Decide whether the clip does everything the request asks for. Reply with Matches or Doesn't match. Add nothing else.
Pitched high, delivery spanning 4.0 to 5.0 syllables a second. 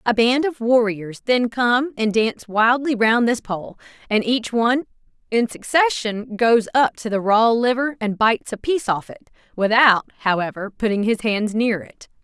Matches